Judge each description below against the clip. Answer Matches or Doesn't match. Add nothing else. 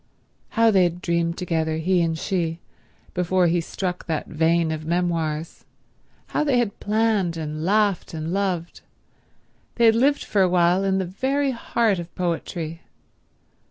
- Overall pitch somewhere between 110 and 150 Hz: Doesn't match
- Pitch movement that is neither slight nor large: Matches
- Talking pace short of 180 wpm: Matches